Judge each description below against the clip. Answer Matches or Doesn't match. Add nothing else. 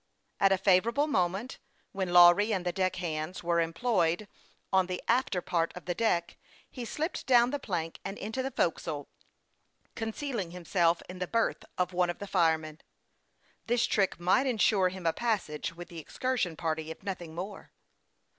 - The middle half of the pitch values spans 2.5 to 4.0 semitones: Doesn't match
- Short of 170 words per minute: Doesn't match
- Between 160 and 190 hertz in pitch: Matches